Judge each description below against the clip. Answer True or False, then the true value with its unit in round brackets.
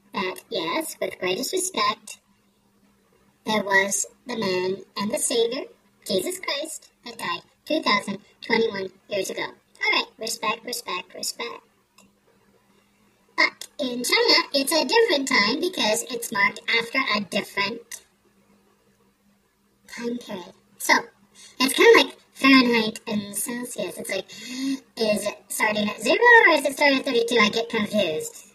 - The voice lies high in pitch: True (235 Hz)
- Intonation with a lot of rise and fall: True (6.3 semitones)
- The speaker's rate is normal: False (130 wpm)